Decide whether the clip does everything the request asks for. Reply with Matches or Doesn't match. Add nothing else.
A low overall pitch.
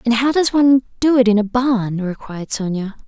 Doesn't match